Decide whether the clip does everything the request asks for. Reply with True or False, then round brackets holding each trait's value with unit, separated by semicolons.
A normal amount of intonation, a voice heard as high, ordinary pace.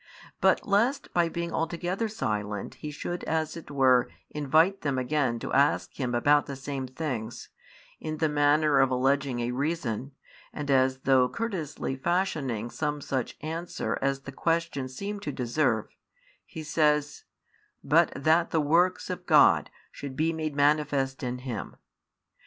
False (3.7 semitones; 145 Hz; 150 wpm)